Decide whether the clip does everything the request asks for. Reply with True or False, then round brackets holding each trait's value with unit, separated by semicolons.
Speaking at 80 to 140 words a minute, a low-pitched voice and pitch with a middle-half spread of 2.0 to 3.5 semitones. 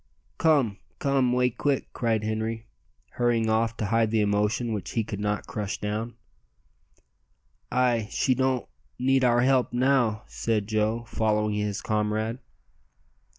True (135 wpm; 115 Hz; 2.6 semitones)